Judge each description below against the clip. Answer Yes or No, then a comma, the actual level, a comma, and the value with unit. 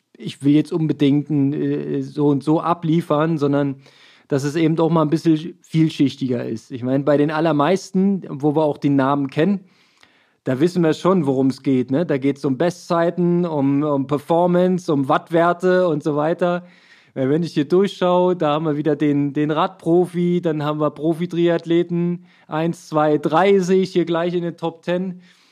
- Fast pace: No, average, 180 wpm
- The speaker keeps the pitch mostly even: No, average, 3.2 semitones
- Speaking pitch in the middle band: Yes, medium, 160 Hz